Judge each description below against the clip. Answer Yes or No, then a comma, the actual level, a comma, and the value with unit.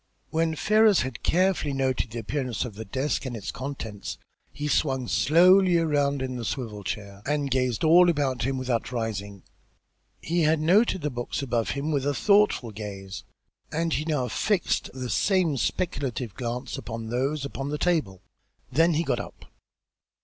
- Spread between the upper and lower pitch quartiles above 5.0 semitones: Yes, wide, 5.4 semitones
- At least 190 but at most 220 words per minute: No, average, 165 wpm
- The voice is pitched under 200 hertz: Yes, low, 135 Hz